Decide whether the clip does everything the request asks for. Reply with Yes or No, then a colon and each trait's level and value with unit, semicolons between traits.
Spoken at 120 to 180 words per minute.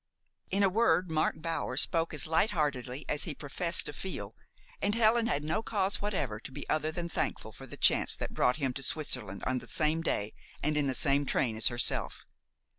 No: average, 200 wpm